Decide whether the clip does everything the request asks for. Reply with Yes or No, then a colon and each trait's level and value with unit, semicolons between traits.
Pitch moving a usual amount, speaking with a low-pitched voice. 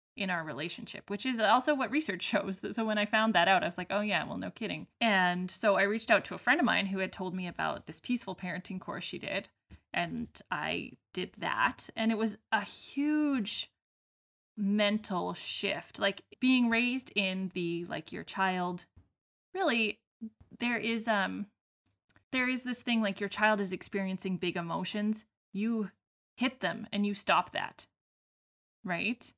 No: average, 3.4 semitones; high, 205 Hz